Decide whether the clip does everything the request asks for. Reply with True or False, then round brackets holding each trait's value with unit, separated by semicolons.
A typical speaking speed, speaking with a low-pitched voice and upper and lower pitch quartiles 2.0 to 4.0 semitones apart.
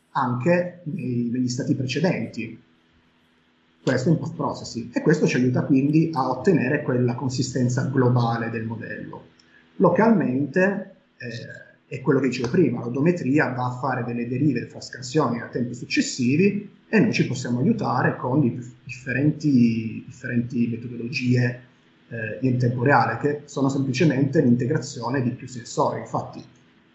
True (140 wpm; 125 Hz; 3.5 semitones)